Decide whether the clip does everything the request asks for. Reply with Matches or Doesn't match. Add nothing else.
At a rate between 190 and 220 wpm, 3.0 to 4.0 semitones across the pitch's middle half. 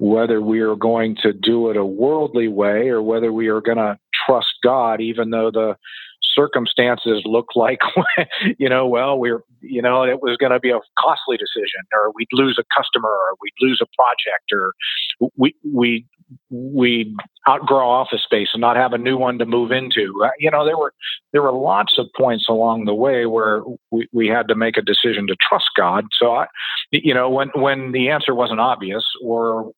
Doesn't match